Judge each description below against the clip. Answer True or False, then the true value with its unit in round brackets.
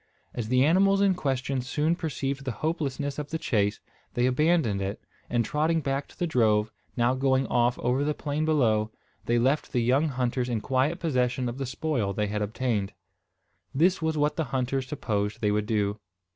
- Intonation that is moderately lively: True (4.3 semitones)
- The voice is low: True (130 Hz)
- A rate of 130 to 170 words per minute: False (185 wpm)